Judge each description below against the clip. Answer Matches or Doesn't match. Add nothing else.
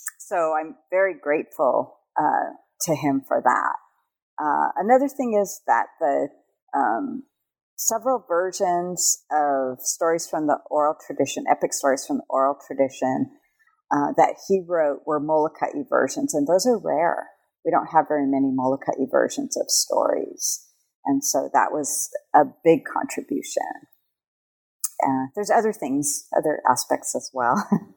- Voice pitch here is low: Doesn't match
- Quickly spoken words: Doesn't match